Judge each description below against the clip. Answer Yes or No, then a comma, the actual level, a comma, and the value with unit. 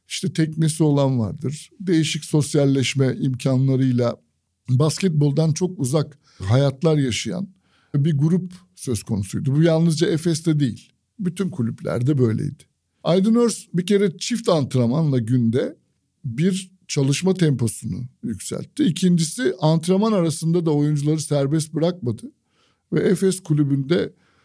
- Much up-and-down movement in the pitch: No, average, 4.8 semitones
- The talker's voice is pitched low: No, medium, 155 Hz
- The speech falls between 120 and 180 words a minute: No, average, 110 wpm